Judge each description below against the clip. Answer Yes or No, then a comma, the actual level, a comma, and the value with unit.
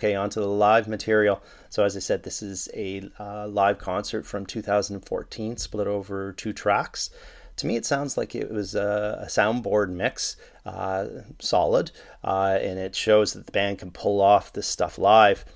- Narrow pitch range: Yes, narrow, 1.4 semitones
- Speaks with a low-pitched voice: Yes, low, 100 Hz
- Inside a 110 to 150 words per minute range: No, average, 175 wpm